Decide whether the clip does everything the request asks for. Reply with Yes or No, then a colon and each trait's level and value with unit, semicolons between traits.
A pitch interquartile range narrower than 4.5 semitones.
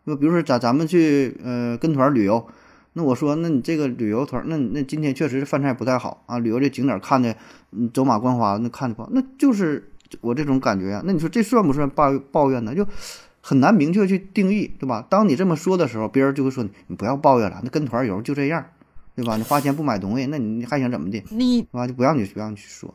No: average, 4.8 semitones